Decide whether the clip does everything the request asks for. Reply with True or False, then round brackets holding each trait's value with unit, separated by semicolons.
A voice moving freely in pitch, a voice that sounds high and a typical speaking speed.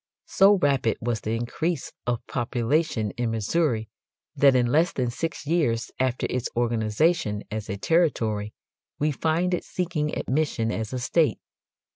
False (5.9 semitones; 125 Hz; 145 wpm)